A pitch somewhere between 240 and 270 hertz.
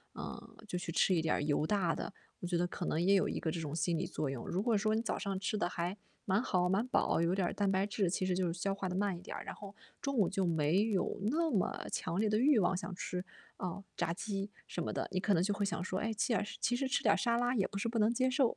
No: high, 195 Hz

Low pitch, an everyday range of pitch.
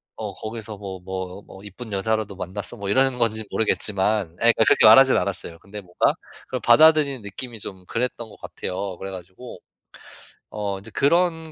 Yes: low, 105 Hz; average, 3.8 semitones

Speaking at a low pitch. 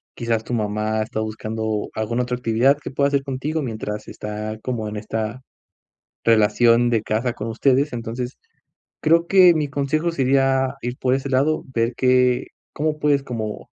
Yes: low, 125 Hz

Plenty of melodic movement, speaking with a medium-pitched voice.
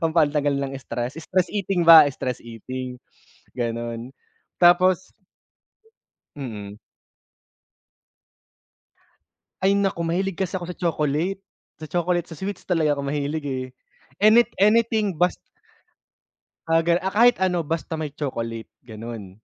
Yes: wide, 6.0 semitones; medium, 160 Hz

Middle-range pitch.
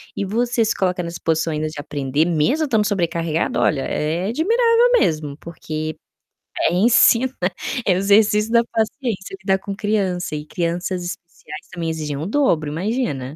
Yes: medium, 180 Hz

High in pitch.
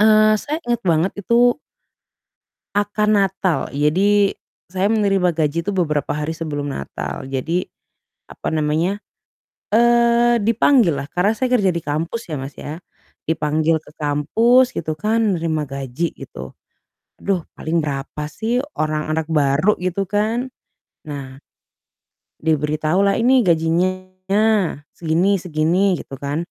No: medium, 175 Hz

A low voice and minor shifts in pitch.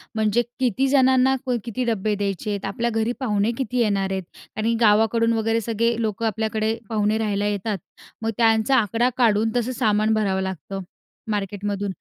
No: high, 220 Hz; narrow, 2.1 semitones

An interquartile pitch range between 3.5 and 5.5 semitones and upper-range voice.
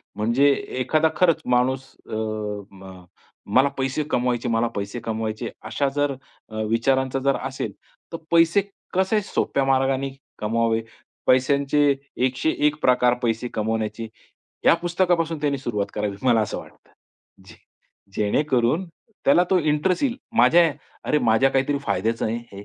No: average, 4.6 semitones; low, 130 Hz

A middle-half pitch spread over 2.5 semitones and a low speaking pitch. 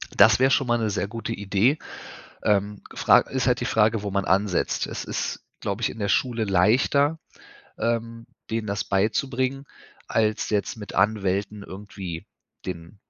Yes: average, 2.9 semitones; low, 105 Hz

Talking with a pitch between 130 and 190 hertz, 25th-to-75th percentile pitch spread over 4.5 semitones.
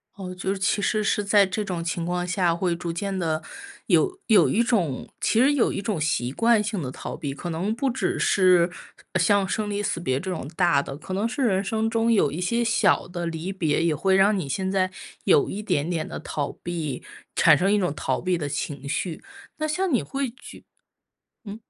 No: medium, 185 Hz; average, 4.2 semitones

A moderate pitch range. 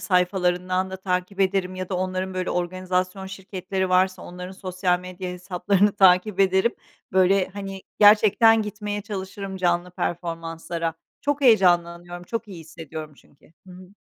No: narrow, 1.5 semitones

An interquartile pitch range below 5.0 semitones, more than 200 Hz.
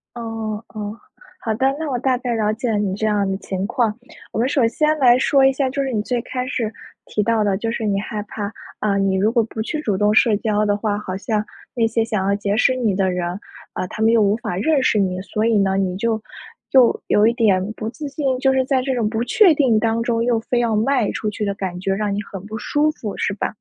Yes: average, 3.2 semitones; high, 220 Hz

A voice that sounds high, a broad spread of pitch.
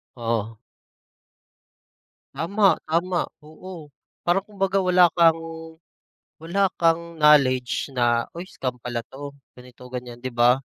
No: medium, 150 Hz; wide, 5.8 semitones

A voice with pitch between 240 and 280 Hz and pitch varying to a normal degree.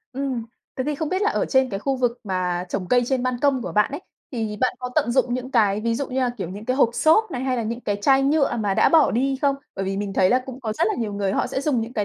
Yes: high, 245 Hz; average, 4.2 semitones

